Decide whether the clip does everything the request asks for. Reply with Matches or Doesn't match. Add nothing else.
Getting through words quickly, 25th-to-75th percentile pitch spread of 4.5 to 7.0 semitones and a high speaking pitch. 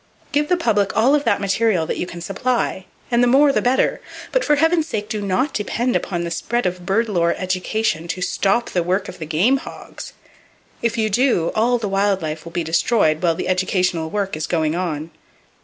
Matches